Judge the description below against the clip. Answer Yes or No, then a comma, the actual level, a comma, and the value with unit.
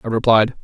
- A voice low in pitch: Yes, low, 110 Hz